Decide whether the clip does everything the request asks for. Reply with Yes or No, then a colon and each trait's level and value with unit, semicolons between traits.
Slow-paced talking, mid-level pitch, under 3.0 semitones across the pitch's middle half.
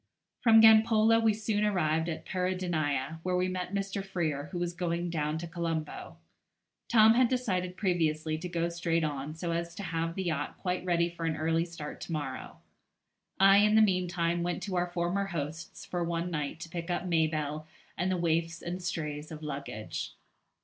No: average, 185 wpm; medium, 170 Hz; narrow, 2.5 semitones